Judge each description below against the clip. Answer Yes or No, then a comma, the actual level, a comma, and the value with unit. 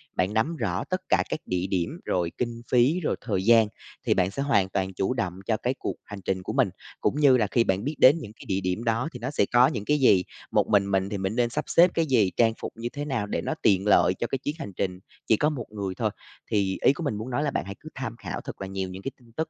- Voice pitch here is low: Yes, low, 110 Hz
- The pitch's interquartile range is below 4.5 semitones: No, average, 5.1 semitones